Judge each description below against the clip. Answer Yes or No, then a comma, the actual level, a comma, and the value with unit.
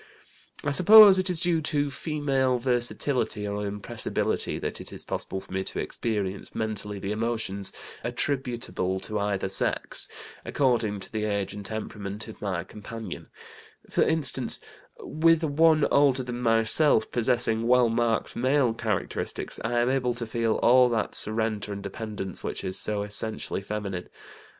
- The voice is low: Yes, low, 115 Hz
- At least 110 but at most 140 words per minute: No, average, 150 wpm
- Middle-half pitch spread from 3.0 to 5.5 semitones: Yes, average, 4.2 semitones